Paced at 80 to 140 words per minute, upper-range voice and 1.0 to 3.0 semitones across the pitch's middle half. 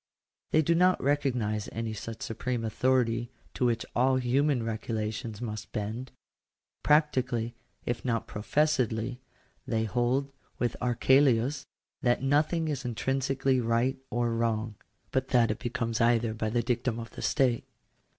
No: slow, 135 wpm; low, 120 Hz; narrow, 2.6 semitones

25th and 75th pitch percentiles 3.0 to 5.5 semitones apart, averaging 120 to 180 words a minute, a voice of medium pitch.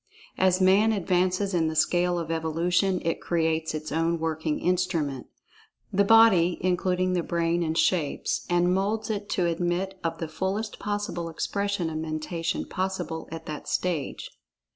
No: narrow, 2.6 semitones; average, 150 wpm; medium, 175 Hz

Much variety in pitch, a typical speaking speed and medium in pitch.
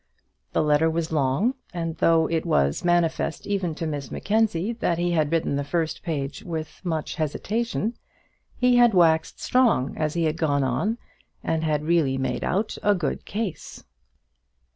No: average, 3.4 semitones; average, 165 wpm; medium, 165 Hz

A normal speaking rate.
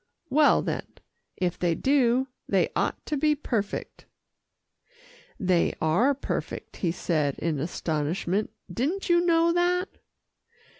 No: slow, 115 wpm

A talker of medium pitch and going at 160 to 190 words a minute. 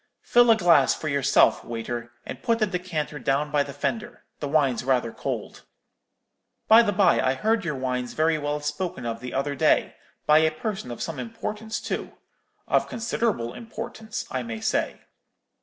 Yes: medium, 150 Hz; average, 170 wpm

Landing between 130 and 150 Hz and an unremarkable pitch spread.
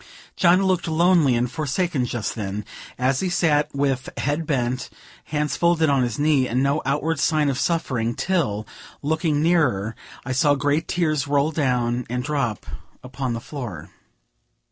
Yes: medium, 140 Hz; average, 4.1 semitones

